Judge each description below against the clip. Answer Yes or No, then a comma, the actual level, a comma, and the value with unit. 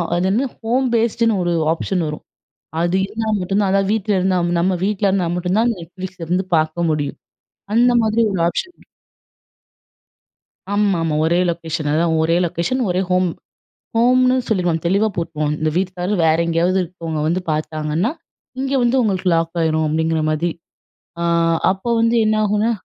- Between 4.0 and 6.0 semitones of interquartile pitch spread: Yes, average, 4.3 semitones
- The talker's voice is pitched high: No, medium, 180 Hz